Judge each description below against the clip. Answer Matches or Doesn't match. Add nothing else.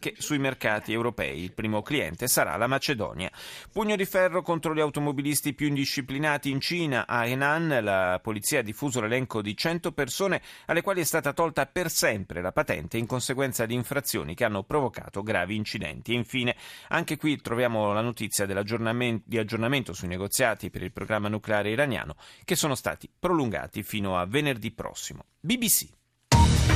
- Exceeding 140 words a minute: Matches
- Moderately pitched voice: Doesn't match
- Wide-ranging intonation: Matches